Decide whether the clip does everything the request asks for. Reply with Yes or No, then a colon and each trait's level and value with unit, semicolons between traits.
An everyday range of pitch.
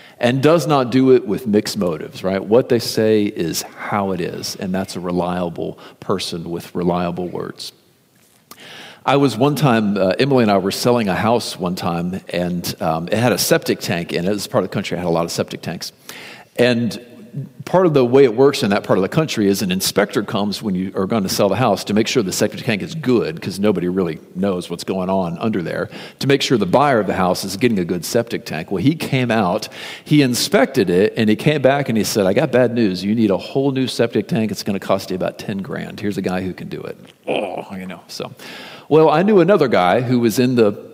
No: wide, 6.2 semitones